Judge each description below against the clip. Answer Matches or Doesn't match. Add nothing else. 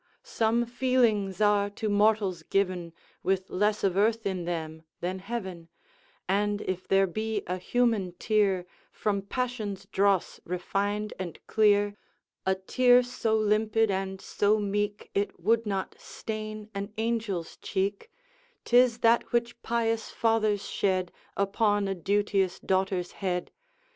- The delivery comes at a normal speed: Doesn't match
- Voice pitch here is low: Doesn't match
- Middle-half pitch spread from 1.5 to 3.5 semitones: Matches